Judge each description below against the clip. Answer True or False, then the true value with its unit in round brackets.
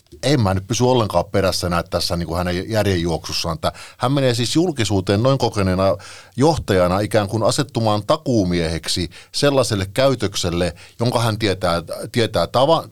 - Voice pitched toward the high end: False (100 Hz)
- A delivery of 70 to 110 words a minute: False (135 wpm)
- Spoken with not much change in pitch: False (5.2 semitones)